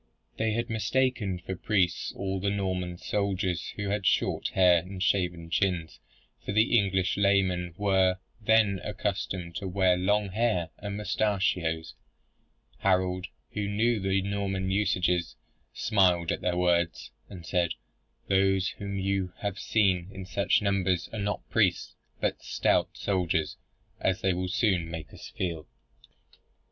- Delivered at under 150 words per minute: Yes, average, 140 wpm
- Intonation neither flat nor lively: No, narrow, 2.1 semitones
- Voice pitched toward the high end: No, very low, 95 Hz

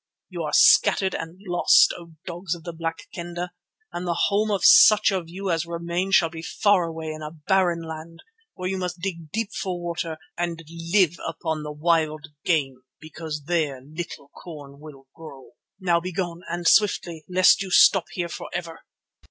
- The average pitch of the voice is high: No, medium, 170 Hz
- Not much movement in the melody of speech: Yes, narrow, 2.2 semitones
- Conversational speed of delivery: Yes, average, 175 wpm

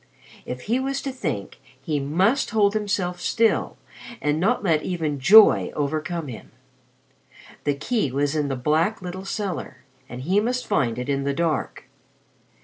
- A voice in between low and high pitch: Yes, medium, 165 Hz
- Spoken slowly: No, average, 155 wpm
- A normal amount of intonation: No, wide, 6.6 semitones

